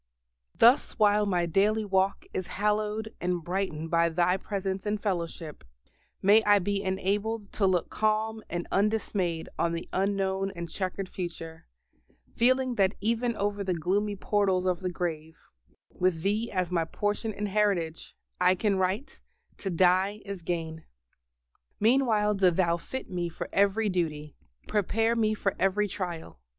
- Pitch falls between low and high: No, high, 195 Hz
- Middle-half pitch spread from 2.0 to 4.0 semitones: Yes, average, 3.0 semitones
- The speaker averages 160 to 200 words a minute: No, average, 150 wpm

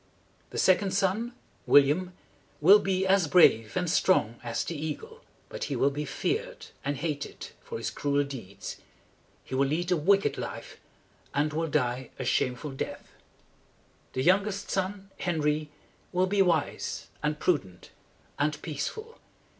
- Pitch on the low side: No, medium, 160 Hz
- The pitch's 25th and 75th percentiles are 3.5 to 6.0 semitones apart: Yes, average, 5.2 semitones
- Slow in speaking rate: No, average, 145 wpm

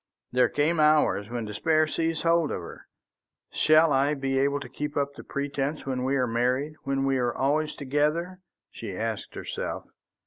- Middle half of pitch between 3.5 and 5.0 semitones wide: No, average, 2.7 semitones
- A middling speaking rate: Yes, average, 175 wpm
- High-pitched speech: No, medium, 140 Hz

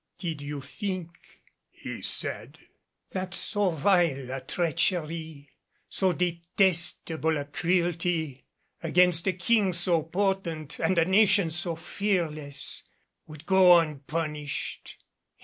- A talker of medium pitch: Yes, medium, 170 Hz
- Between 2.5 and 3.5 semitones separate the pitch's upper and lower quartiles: Yes, average, 3.0 semitones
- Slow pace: Yes, slow, 105 wpm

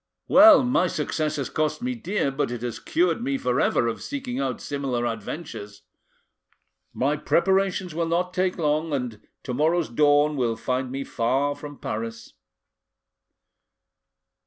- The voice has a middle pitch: Yes, medium, 150 Hz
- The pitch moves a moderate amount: No, wide, 6.3 semitones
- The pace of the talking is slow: No, average, 145 wpm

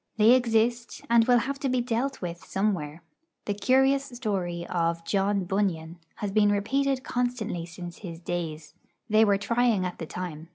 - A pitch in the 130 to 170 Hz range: No, high, 205 Hz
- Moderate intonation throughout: No, wide, 5.7 semitones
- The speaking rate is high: No, average, 165 wpm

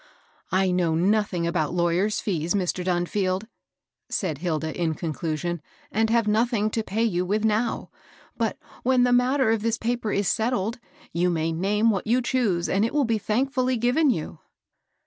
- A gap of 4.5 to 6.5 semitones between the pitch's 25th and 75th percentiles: Yes, average, 4.8 semitones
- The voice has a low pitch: No, high, 205 Hz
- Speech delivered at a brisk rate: No, average, 185 wpm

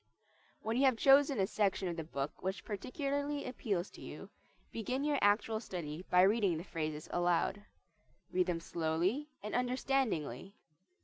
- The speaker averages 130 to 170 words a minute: Yes, average, 150 wpm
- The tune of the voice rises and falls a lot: Yes, wide, 6.6 semitones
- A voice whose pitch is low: No, high, 200 Hz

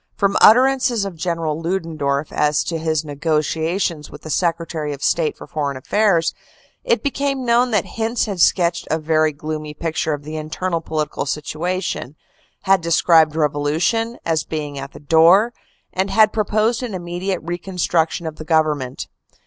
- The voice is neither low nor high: Yes, medium, 165 Hz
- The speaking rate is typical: Yes, average, 155 wpm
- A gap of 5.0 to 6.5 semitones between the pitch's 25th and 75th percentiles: No, average, 4.1 semitones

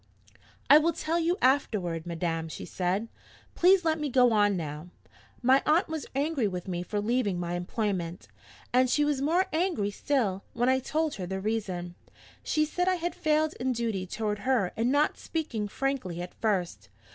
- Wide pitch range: Yes, wide, 8.4 semitones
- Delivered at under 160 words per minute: No, average, 180 wpm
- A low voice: No, high, 230 Hz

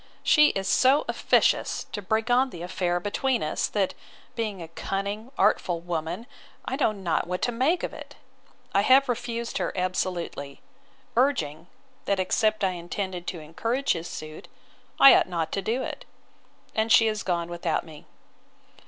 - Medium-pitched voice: No, high, 195 Hz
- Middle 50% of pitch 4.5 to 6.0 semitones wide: Yes, average, 5.2 semitones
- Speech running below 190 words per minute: Yes, average, 160 wpm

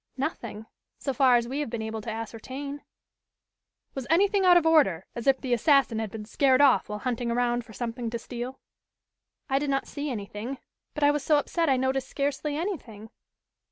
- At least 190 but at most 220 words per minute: Yes, average, 195 wpm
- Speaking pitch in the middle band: No, very high, 260 Hz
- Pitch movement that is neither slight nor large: Yes, average, 3.9 semitones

